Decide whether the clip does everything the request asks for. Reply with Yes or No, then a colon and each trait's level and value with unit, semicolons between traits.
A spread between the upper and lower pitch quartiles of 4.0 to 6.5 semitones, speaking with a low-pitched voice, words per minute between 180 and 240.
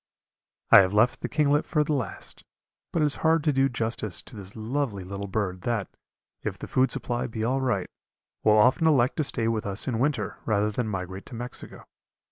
Yes: average, 4.8 semitones; low, 115 Hz; fast, 205 wpm